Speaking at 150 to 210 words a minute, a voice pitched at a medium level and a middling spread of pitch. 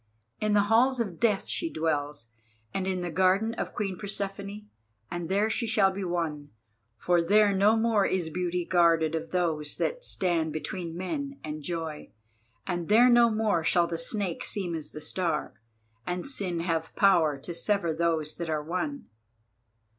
Yes: average, 170 wpm; medium, 180 Hz; average, 4.0 semitones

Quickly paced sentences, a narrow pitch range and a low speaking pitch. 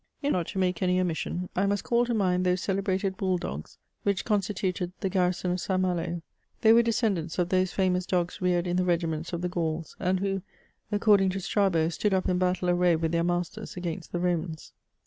No: fast, 210 wpm; narrow, 1.7 semitones; medium, 180 Hz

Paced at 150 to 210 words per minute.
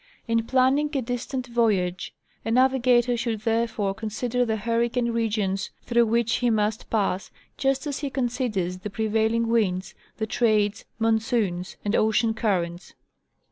No: average, 140 wpm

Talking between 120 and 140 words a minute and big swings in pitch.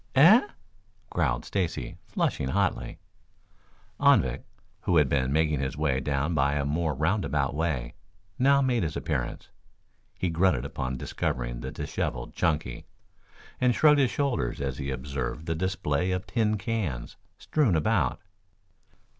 Yes: slow, 135 wpm; wide, 6.1 semitones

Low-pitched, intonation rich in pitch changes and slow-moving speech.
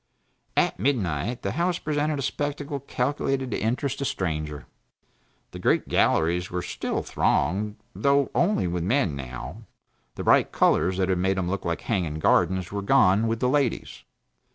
No: low, 105 Hz; wide, 7.7 semitones; average, 160 wpm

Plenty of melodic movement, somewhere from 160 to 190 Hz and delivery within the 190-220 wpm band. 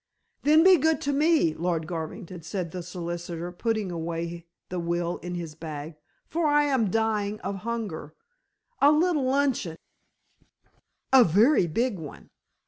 No: wide, 7.7 semitones; medium, 185 Hz; average, 145 wpm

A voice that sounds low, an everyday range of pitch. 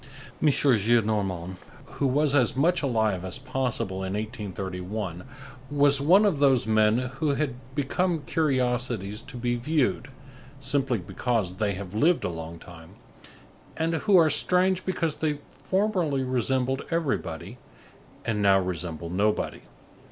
No: low, 125 Hz; wide, 6.6 semitones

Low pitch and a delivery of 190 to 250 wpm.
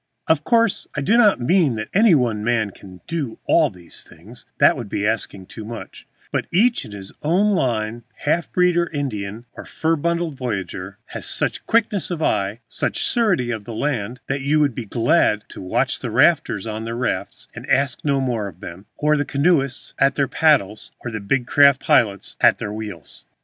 Yes: low, 125 Hz; average, 195 wpm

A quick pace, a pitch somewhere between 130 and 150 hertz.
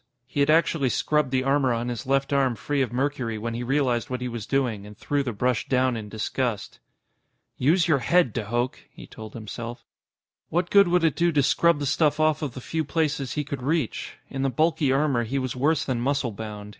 Yes: fast, 220 wpm; low, 135 Hz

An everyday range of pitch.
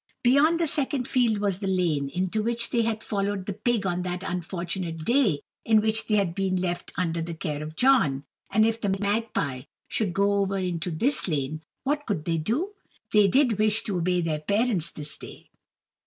Yes: average, 4.7 semitones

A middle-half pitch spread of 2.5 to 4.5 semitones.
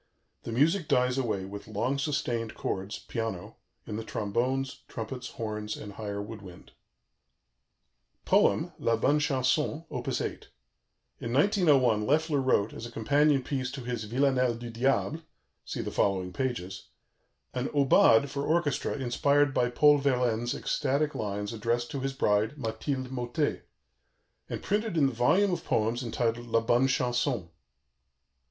Yes: average, 3.8 semitones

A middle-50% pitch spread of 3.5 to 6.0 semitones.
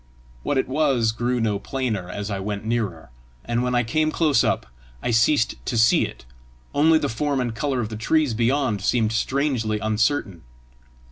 Yes: average, 4.1 semitones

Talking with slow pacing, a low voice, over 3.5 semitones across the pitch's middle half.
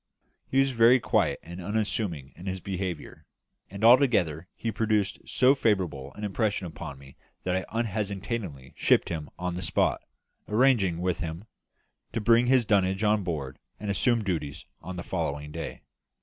No: average, 160 wpm; very low, 95 Hz; average, 4.8 semitones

